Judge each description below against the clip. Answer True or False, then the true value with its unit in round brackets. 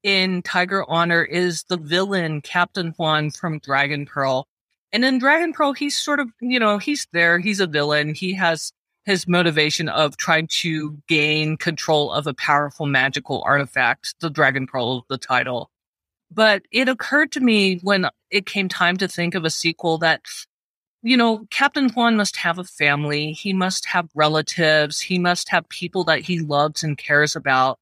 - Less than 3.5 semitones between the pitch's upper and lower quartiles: False (4.4 semitones)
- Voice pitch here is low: False (170 Hz)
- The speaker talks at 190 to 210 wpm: False (175 wpm)